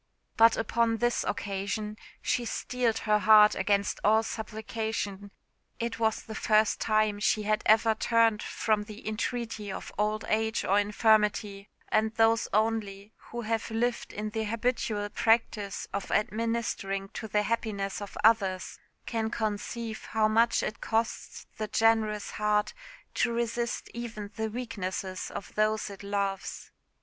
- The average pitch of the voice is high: Yes, high, 215 Hz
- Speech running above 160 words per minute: No, average, 140 wpm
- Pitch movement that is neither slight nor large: No, narrow, 1.6 semitones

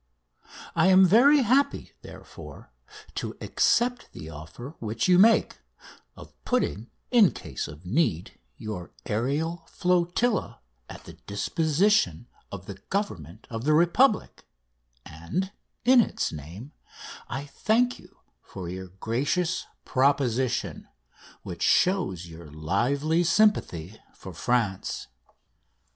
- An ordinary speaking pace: No, slow, 110 wpm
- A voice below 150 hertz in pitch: Yes, medium, 140 Hz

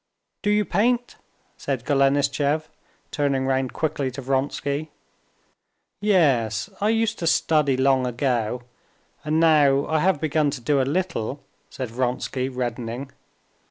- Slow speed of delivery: Yes, slow, 125 wpm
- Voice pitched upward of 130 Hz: Yes, medium, 140 Hz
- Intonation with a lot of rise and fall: No, average, 3.4 semitones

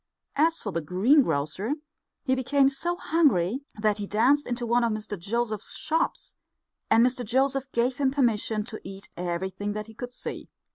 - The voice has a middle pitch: No, high, 235 Hz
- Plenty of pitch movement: No, average, 4.6 semitones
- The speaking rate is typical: Yes, average, 165 wpm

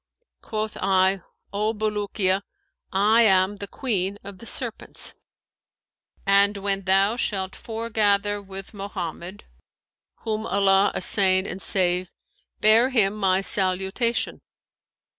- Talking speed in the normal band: No, slow, 105 wpm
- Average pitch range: No, narrow, 2.0 semitones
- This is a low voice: No, high, 200 Hz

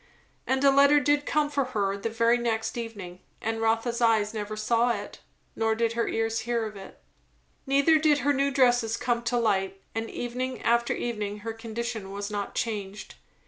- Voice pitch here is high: Yes, high, 230 Hz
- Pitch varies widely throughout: No, narrow, 2.5 semitones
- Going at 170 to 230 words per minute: Yes, average, 185 wpm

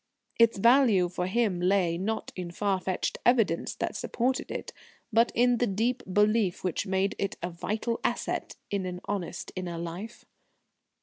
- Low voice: No, high, 195 Hz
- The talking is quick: No, average, 160 wpm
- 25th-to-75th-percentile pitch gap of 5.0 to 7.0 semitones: No, average, 4.2 semitones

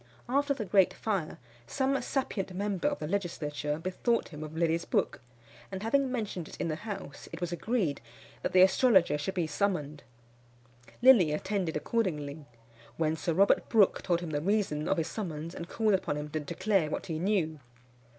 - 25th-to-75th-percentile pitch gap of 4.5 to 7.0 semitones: Yes, average, 5.1 semitones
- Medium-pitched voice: Yes, medium, 180 Hz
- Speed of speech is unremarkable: Yes, average, 180 wpm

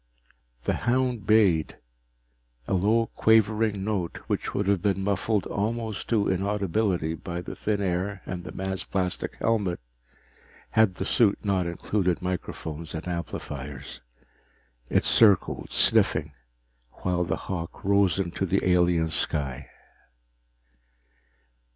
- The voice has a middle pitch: No, very low, 95 Hz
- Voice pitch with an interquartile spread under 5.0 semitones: Yes, average, 3.0 semitones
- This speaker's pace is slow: Yes, slow, 120 wpm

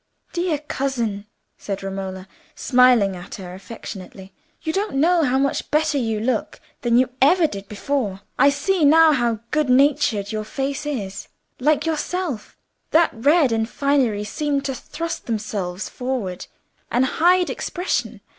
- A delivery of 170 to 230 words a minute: No, average, 145 wpm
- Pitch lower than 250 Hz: No, very high, 260 Hz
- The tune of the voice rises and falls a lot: Yes, wide, 6.1 semitones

